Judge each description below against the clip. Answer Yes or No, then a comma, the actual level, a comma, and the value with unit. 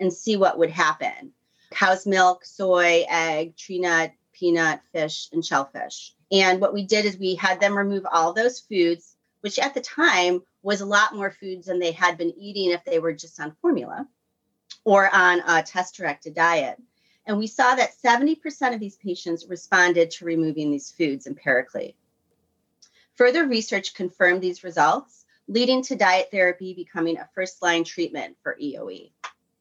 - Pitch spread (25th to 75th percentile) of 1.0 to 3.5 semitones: No, average, 4.0 semitones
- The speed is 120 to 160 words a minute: No, average, 170 wpm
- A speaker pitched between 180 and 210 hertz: Yes, medium, 185 Hz